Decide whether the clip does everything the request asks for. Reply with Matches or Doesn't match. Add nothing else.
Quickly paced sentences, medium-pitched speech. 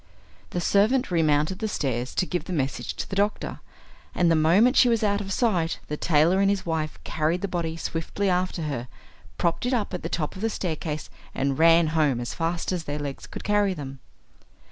Matches